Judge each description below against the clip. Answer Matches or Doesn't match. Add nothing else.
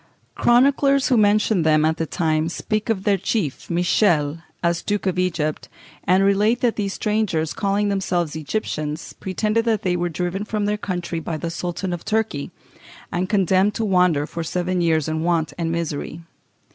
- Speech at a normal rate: Matches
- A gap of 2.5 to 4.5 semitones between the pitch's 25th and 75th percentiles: Matches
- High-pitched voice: Doesn't match